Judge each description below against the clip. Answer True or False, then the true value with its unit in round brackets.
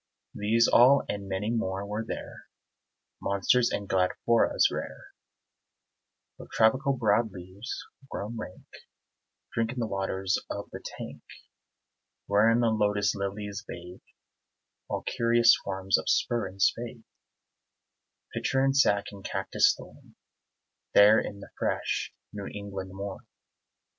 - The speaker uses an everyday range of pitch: True (3.0 semitones)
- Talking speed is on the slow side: True (120 wpm)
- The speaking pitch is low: True (105 Hz)